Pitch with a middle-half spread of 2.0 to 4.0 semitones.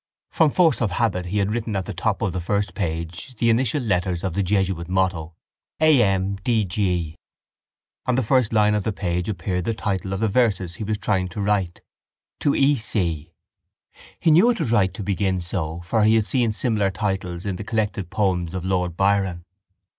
Yes: average, 3.4 semitones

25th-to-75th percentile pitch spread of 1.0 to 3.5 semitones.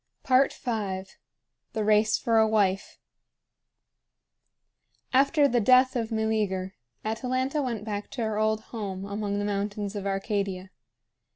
Yes: average, 2.7 semitones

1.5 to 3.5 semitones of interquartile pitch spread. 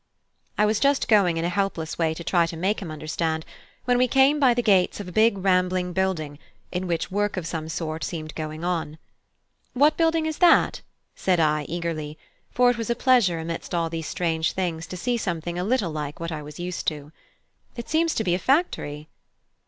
No: average, 5.3 semitones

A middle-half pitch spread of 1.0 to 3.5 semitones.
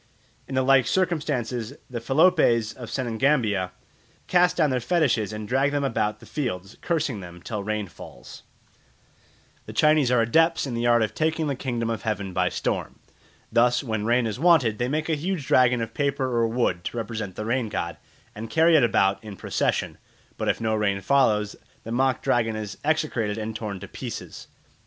No: average, 4.6 semitones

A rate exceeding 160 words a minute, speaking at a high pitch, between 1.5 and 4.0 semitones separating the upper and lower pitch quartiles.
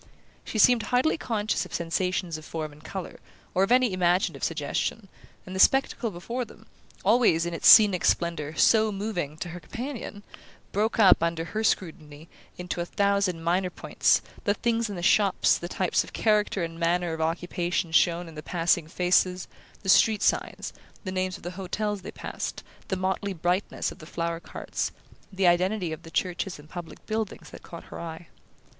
No: average, 180 wpm; medium, 180 Hz; average, 3.6 semitones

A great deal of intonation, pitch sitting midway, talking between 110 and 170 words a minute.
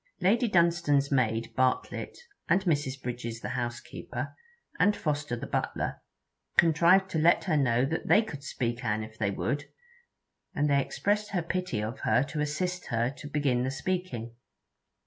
Yes: wide, 5.9 semitones; medium, 145 Hz; average, 160 wpm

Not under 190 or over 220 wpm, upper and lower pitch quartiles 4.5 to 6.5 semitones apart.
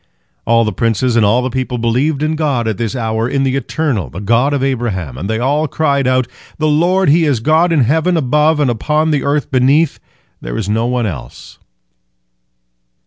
Yes: average, 195 wpm; average, 4.8 semitones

